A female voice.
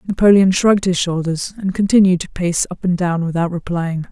Yes: female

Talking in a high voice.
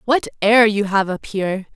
Yes: high, 210 Hz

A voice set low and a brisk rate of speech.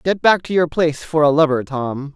No: medium, 155 Hz; fast, 250 wpm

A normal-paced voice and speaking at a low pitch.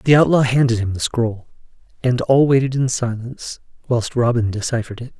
Yes: average, 175 wpm; low, 120 Hz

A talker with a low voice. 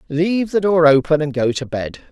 No: medium, 155 Hz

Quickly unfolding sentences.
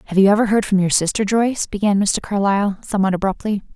Yes: fast, 210 wpm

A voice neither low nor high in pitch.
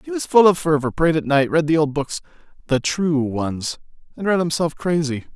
Yes: medium, 155 Hz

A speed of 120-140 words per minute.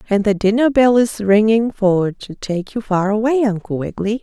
No: average, 200 wpm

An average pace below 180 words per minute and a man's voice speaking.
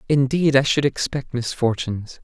Yes: slow, 135 wpm; male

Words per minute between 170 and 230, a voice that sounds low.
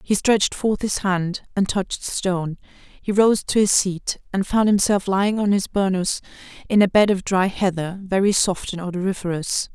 No: average, 185 wpm; high, 190 Hz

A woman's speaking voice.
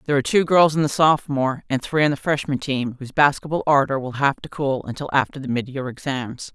Yes: female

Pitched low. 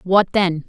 No: medium, 185 Hz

